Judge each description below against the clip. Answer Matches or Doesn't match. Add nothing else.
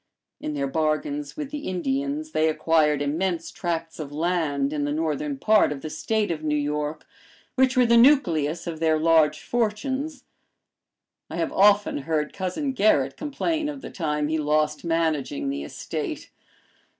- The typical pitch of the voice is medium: Matches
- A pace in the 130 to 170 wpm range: Matches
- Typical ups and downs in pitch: Doesn't match